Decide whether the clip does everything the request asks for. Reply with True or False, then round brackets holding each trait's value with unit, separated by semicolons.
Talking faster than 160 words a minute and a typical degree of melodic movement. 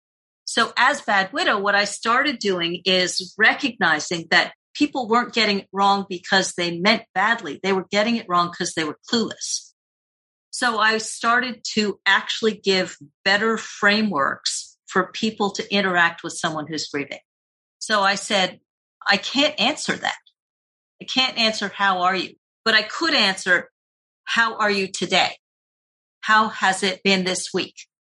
False (155 wpm; 3.1 semitones)